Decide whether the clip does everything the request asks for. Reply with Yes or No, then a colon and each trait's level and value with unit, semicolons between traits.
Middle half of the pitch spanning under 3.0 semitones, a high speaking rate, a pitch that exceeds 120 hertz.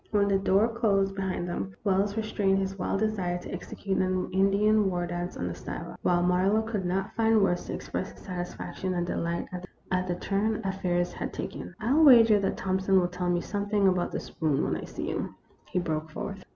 Yes: narrow, 2.5 semitones; fast, 215 wpm; high, 190 Hz